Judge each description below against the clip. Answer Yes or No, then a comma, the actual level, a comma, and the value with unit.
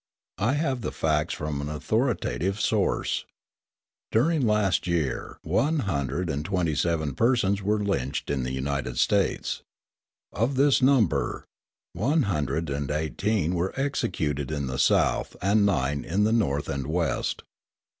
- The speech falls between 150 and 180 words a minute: No, average, 140 wpm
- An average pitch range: No, wide, 7.1 semitones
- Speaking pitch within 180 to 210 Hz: No, very low, 85 Hz